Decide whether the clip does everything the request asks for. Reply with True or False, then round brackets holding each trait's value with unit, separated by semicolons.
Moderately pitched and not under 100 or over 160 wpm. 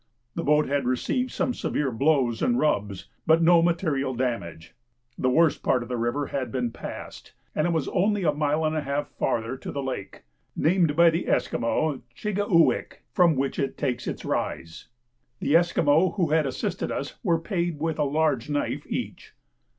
False (150 Hz; 185 wpm)